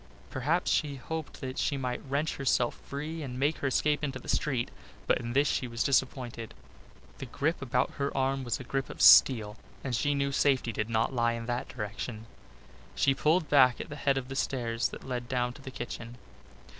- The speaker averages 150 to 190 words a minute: No, fast, 205 wpm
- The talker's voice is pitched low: Yes, low, 130 Hz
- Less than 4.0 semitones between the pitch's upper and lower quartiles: Yes, narrow, 2.6 semitones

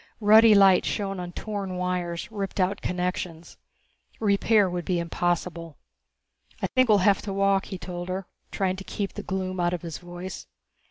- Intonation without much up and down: Yes, narrow, 2.1 semitones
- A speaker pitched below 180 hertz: No, medium, 185 Hz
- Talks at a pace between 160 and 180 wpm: Yes, average, 170 wpm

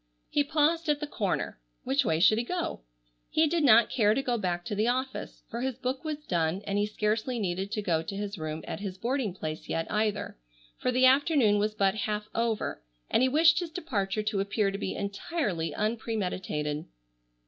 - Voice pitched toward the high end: Yes, high, 215 Hz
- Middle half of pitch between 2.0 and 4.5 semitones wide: No, average, 5.1 semitones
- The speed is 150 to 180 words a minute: No, average, 200 wpm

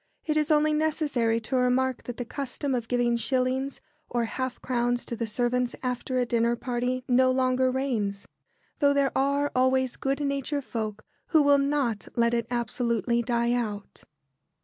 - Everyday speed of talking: Yes, average, 165 wpm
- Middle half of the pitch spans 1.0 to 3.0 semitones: Yes, narrow, 2.4 semitones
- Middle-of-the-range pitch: No, very high, 250 Hz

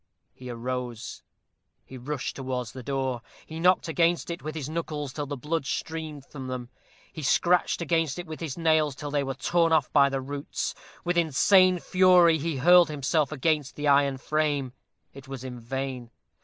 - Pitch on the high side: No, medium, 145 Hz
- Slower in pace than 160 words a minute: No, average, 180 wpm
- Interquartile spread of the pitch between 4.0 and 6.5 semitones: No, average, 3.6 semitones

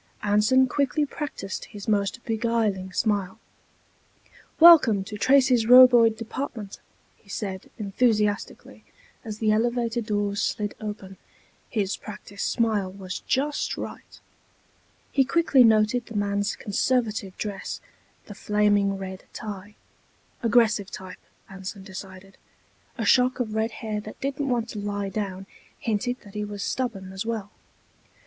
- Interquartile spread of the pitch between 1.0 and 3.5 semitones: Yes, average, 2.9 semitones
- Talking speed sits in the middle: No, slow, 125 wpm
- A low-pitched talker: No, high, 215 Hz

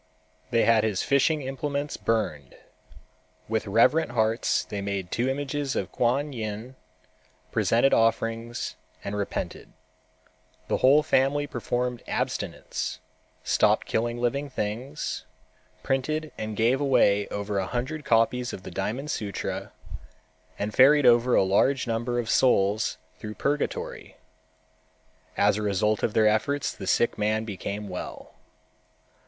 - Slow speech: Yes, slow, 125 wpm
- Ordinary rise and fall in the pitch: Yes, average, 4.1 semitones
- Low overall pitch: Yes, low, 115 Hz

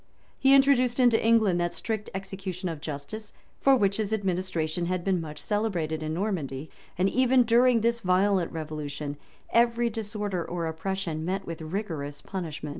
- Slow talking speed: No, average, 160 wpm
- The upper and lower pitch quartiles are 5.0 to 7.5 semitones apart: Yes, wide, 5.5 semitones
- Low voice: No, high, 190 Hz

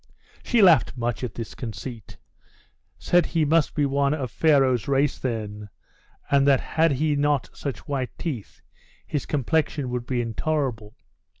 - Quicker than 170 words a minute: No, average, 145 wpm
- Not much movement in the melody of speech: No, average, 3.7 semitones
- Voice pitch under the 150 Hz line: Yes, low, 135 Hz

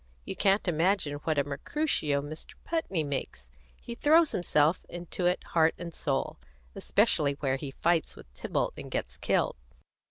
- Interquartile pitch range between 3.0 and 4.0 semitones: No, average, 4.6 semitones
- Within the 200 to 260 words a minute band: No, average, 155 wpm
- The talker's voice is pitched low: No, medium, 160 Hz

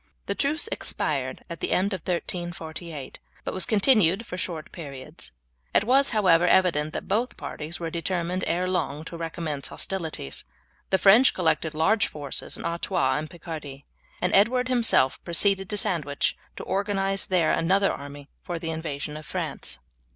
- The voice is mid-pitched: Yes, medium, 175 Hz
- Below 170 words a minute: Yes, average, 160 wpm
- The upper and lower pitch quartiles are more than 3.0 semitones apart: Yes, average, 3.8 semitones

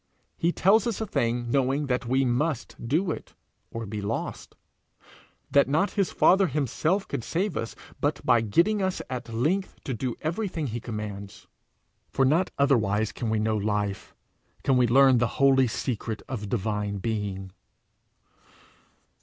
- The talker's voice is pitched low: Yes, low, 125 Hz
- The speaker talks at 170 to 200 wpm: No, average, 155 wpm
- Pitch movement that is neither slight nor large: No, wide, 5.9 semitones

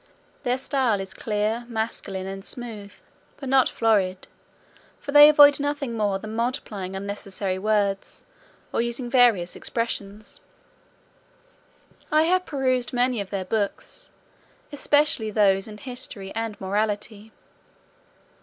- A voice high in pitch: Yes, high, 220 Hz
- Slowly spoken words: Yes, slow, 115 wpm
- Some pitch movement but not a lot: Yes, average, 4.0 semitones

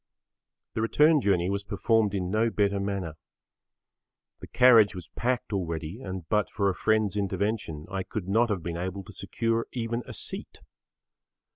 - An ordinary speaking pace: Yes, average, 160 wpm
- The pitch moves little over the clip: No, average, 3.3 semitones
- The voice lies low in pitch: Yes, low, 100 Hz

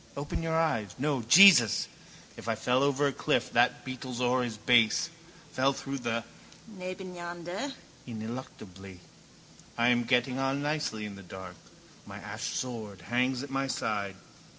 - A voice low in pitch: Yes, low, 125 Hz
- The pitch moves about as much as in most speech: Yes, average, 4.3 semitones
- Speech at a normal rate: Yes, average, 150 wpm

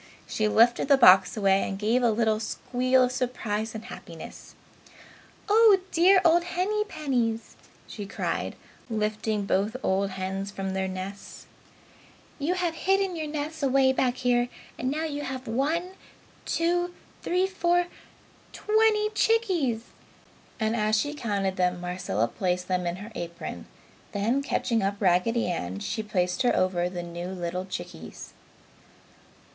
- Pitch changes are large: Yes, wide, 7.8 semitones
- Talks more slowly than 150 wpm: Yes, average, 140 wpm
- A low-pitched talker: No, high, 225 Hz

